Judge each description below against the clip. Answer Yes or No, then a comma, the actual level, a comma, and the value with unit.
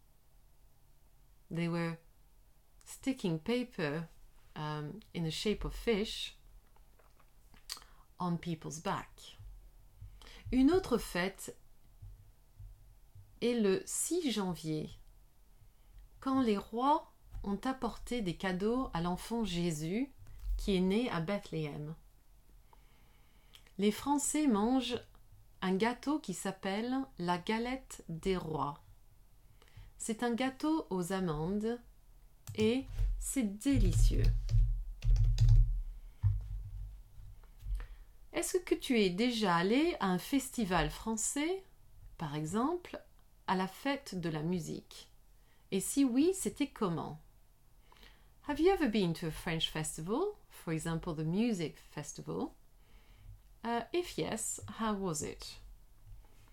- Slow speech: Yes, slow, 100 wpm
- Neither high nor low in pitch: Yes, medium, 175 Hz